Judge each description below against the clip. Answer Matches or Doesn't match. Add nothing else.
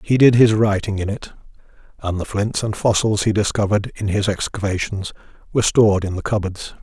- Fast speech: Doesn't match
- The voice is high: Doesn't match